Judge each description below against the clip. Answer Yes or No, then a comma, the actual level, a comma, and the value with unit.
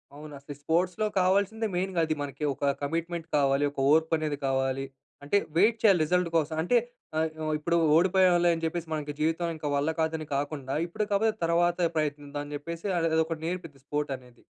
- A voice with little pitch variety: No, average, 3.2 semitones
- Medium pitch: Yes, medium, 160 Hz